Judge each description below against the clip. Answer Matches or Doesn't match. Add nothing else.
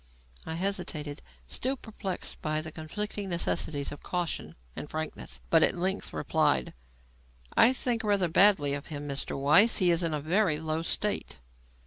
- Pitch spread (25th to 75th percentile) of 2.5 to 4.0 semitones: Doesn't match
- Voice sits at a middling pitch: Matches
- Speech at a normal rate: Matches